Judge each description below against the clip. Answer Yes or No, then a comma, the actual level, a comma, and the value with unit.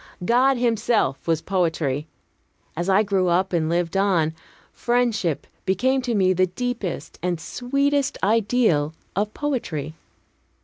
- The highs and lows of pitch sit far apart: Yes, wide, 6.4 semitones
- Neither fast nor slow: No, slow, 125 wpm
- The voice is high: Yes, high, 195 Hz